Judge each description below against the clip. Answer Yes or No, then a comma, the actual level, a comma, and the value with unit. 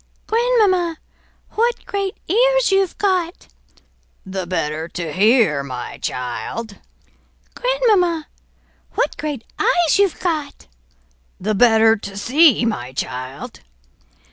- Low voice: No, very high, 290 Hz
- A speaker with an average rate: No, slow, 100 wpm